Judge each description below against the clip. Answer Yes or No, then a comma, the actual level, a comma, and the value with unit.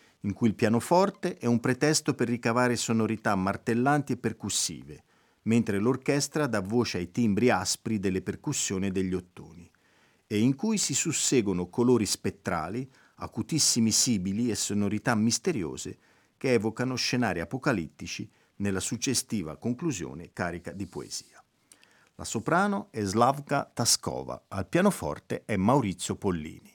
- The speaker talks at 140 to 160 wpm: No, average, 130 wpm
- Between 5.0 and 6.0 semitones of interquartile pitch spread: No, average, 4.3 semitones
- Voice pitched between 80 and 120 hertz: Yes, low, 115 Hz